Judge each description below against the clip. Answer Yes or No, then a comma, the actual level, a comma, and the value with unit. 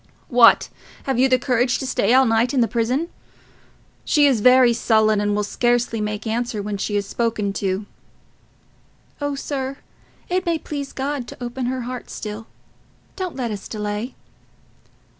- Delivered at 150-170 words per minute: Yes, average, 160 wpm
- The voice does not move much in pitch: No, average, 3.5 semitones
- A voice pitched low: No, high, 240 Hz